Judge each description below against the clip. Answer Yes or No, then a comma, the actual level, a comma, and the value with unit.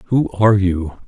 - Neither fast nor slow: Yes, average, 170 wpm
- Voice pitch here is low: Yes, low, 100 Hz